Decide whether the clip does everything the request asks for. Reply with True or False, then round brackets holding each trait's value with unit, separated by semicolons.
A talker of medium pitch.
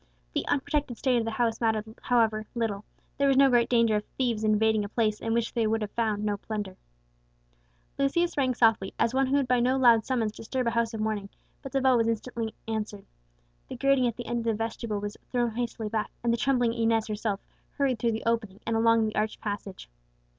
False (230 Hz)